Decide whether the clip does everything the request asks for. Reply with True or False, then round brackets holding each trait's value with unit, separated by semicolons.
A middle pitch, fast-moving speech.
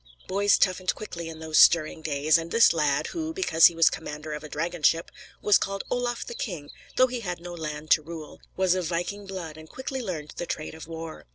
True (170 Hz; 220 wpm)